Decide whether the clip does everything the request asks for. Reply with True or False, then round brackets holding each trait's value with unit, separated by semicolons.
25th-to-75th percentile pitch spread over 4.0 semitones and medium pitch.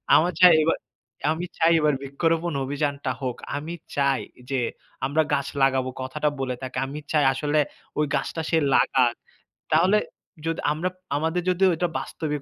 False (3.2 semitones; 150 Hz)